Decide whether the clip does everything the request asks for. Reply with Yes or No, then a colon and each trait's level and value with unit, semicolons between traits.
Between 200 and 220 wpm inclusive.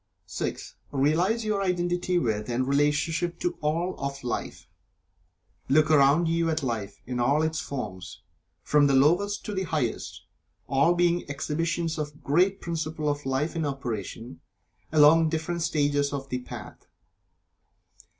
No: average, 140 wpm